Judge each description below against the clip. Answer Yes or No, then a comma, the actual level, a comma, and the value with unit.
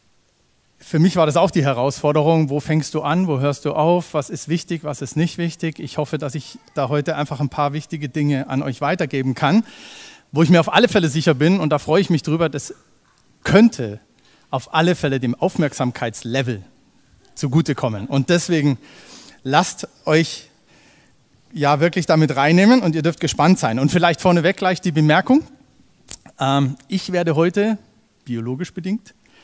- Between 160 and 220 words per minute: Yes, average, 170 wpm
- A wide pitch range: No, average, 3.4 semitones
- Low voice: No, medium, 155 Hz